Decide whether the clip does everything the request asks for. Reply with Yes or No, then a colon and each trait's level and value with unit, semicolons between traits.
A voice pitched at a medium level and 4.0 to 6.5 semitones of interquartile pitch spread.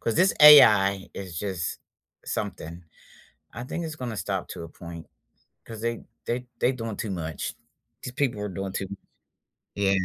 No: low, 105 Hz; average, 4.5 semitones